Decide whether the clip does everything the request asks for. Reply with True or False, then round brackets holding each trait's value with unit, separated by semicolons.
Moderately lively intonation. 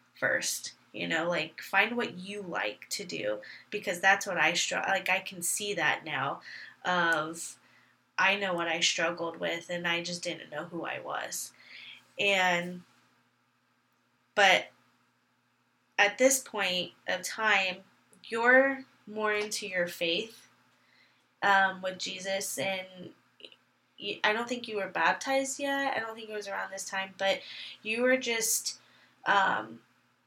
True (3.6 semitones)